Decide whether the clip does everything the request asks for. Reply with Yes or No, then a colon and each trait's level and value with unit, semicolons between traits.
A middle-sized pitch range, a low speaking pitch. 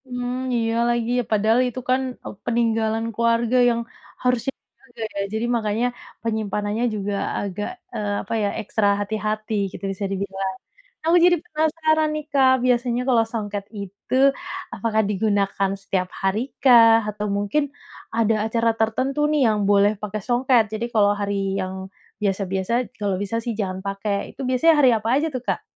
No: average, 3.1 semitones; high, 220 Hz